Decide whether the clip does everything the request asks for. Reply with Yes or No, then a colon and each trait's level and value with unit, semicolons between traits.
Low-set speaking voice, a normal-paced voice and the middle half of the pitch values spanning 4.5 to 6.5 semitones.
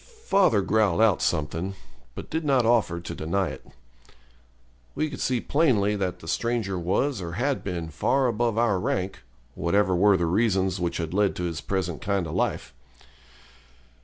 Yes: low, 100 Hz; average, 165 wpm; average, 5.1 semitones